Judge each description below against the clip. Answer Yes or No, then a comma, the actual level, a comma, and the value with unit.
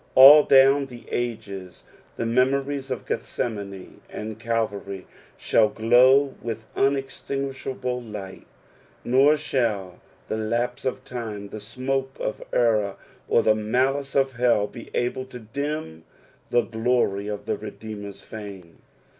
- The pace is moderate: No, slow, 125 wpm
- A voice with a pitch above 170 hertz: No, low, 120 Hz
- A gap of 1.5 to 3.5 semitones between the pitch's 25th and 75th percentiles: No, average, 4.0 semitones